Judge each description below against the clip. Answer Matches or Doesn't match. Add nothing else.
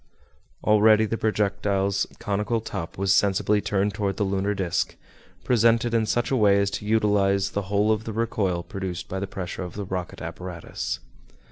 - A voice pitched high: Doesn't match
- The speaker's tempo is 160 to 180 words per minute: Matches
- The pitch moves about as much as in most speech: Doesn't match